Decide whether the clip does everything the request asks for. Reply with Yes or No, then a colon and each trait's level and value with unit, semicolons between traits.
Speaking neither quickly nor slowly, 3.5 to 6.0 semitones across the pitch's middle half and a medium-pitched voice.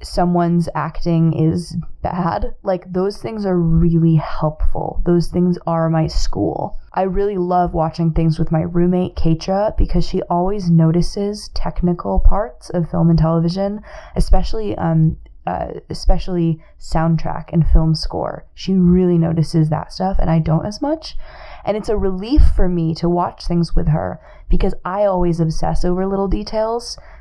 No: average, 155 wpm; narrow, 2.5 semitones; medium, 175 Hz